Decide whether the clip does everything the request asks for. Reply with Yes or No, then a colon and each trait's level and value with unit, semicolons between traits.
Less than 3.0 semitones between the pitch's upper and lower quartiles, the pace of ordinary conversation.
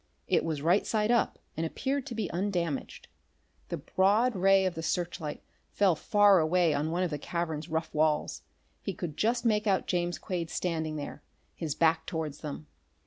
No: average, 3.8 semitones; average, 180 wpm